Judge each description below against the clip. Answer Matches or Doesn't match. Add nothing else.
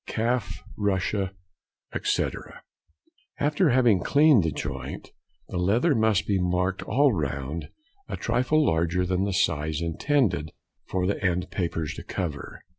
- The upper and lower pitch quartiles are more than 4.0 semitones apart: Matches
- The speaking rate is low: Matches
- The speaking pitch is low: Matches